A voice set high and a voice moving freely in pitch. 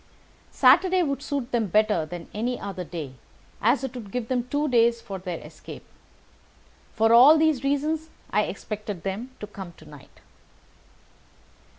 Yes: high, 230 Hz; wide, 5.8 semitones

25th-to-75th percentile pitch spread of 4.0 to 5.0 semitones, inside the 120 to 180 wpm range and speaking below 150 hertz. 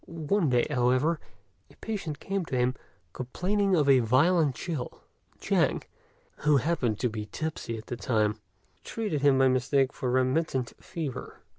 Yes: average, 4.7 semitones; average, 155 wpm; low, 135 Hz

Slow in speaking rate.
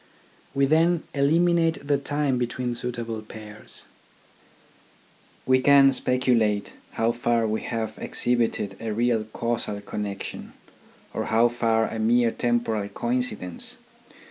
Yes: slow, 115 wpm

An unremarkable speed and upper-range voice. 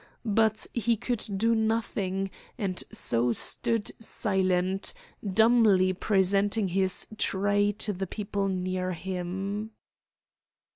No: slow, 100 wpm; high, 200 Hz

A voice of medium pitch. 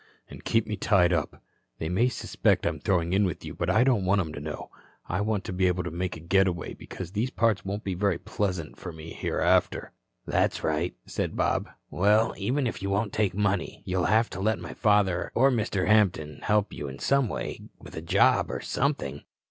No: very low, 95 Hz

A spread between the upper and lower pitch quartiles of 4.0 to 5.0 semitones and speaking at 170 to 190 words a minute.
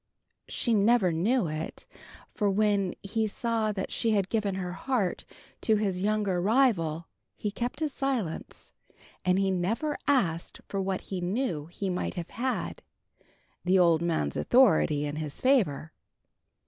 No: average, 4.5 semitones; average, 145 wpm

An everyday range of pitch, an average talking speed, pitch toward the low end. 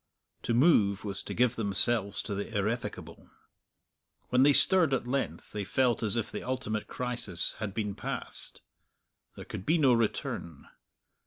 Yes: average, 3.8 semitones; average, 155 wpm; low, 115 Hz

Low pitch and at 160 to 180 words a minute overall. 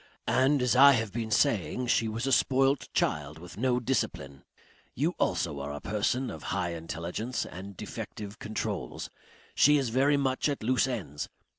Yes: low, 115 Hz; average, 165 wpm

